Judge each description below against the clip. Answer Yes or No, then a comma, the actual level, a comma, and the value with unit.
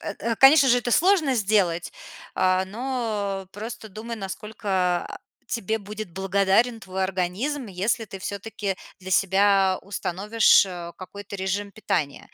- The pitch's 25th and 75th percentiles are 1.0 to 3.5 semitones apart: Yes, average, 2.9 semitones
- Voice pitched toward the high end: Yes, high, 200 Hz